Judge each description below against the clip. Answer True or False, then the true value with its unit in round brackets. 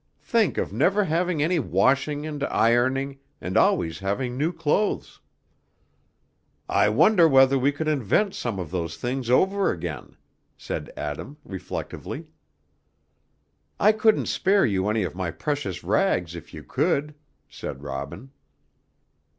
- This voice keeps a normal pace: False (130 wpm)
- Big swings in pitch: True (8.9 semitones)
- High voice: False (135 Hz)